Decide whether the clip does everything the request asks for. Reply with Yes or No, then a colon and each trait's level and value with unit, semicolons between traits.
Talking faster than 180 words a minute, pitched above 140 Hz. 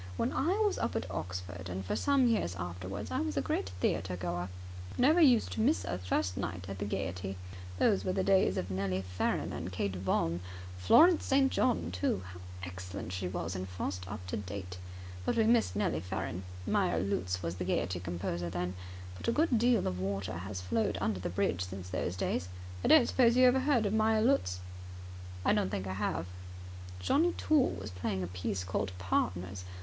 No: average, 200 wpm; very low, 95 Hz